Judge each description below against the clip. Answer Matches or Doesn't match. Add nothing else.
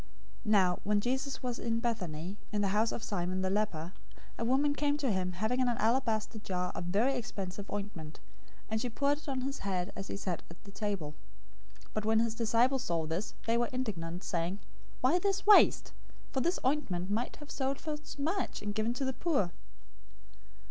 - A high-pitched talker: Matches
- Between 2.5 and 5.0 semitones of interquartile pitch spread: Doesn't match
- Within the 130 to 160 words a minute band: Doesn't match